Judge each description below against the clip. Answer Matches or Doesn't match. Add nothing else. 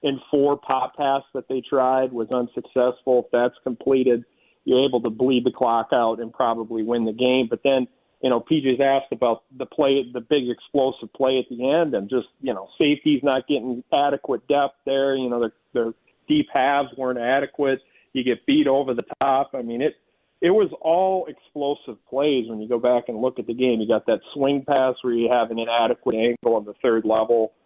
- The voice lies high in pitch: Doesn't match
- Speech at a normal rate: Doesn't match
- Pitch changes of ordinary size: Doesn't match